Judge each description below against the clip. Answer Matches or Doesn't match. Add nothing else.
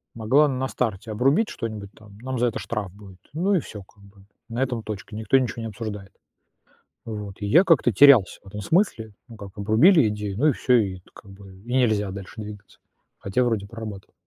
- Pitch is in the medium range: Doesn't match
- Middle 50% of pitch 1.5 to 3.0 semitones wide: Doesn't match